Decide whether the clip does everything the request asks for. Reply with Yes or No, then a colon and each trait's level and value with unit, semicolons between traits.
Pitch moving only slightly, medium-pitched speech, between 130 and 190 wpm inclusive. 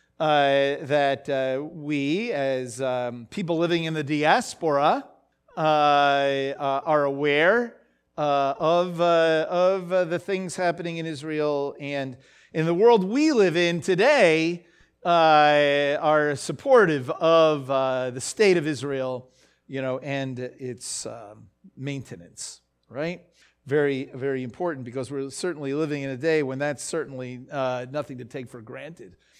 No: average, 3.4 semitones; medium, 145 Hz; average, 140 wpm